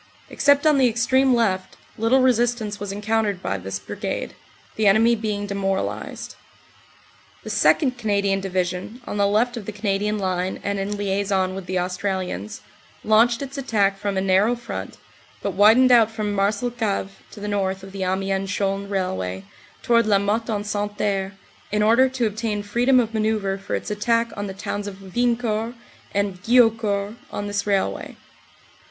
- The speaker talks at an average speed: Yes, average, 160 wpm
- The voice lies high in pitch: Yes, high, 205 Hz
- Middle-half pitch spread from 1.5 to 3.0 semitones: Yes, average, 2.7 semitones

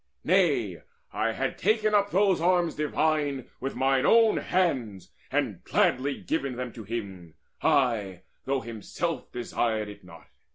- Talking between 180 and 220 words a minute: No, slow, 135 wpm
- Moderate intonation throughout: No, wide, 7.2 semitones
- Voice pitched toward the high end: No, low, 135 Hz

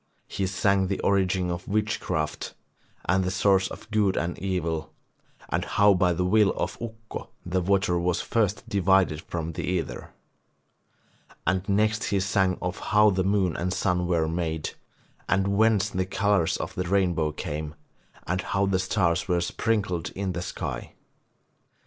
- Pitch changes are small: Yes, narrow, 2.2 semitones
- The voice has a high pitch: No, very low, 95 Hz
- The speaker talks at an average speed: Yes, average, 155 wpm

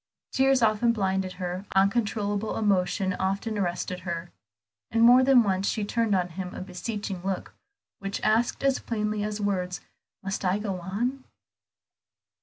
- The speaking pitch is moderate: No, high, 200 Hz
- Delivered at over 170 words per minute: No, average, 145 wpm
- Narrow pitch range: No, average, 3.0 semitones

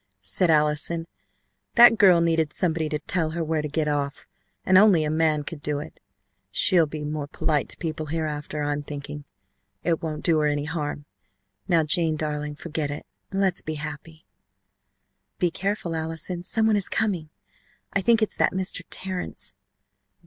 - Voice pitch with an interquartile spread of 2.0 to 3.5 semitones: Yes, average, 2.8 semitones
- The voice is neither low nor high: Yes, medium, 160 Hz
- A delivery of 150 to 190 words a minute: Yes, average, 170 wpm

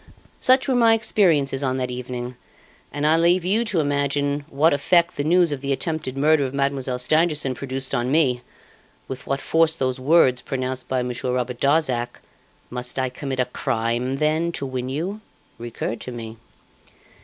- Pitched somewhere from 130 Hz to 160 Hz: Yes, low, 135 Hz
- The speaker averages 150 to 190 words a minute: Yes, average, 170 wpm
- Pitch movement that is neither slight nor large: Yes, average, 3.8 semitones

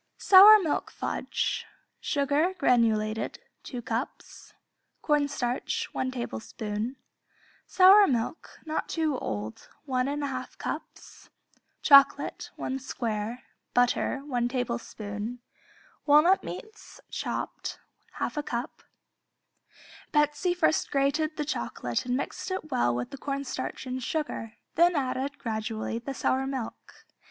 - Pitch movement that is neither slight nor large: Yes, average, 4.1 semitones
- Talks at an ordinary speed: No, slow, 110 wpm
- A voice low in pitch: No, very high, 265 Hz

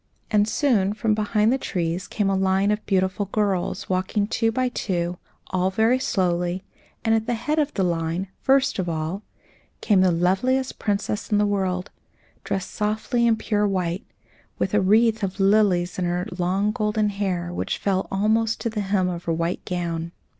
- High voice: Yes, high, 195 Hz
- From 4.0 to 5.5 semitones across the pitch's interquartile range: No, average, 3.1 semitones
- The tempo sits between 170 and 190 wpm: Yes, average, 180 wpm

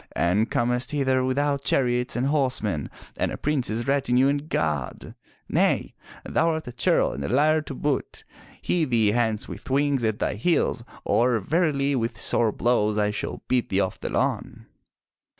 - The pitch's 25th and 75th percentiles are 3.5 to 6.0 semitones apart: Yes, average, 4.3 semitones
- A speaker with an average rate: Yes, average, 170 wpm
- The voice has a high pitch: No, low, 125 Hz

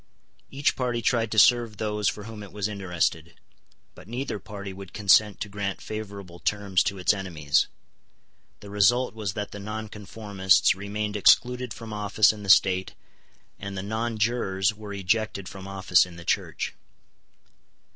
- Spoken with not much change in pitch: Yes, narrow, 2.1 semitones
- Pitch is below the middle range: Yes, low, 105 Hz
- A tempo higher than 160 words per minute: No, average, 155 wpm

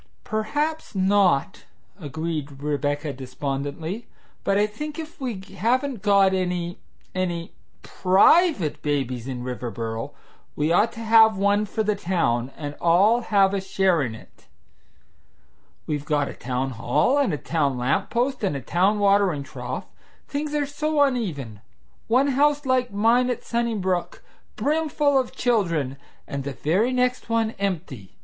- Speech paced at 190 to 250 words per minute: No, average, 140 wpm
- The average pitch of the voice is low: No, high, 190 Hz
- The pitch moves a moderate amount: No, wide, 8.4 semitones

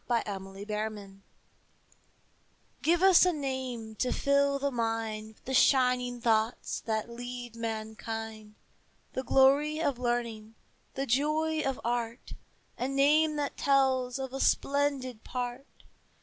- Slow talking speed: Yes, slow, 130 wpm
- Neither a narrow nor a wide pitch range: Yes, average, 3.6 semitones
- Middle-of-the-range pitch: No, very high, 250 Hz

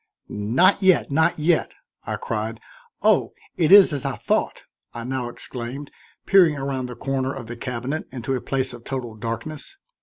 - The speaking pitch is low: Yes, low, 130 Hz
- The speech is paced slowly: No, average, 170 wpm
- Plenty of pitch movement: No, average, 4.3 semitones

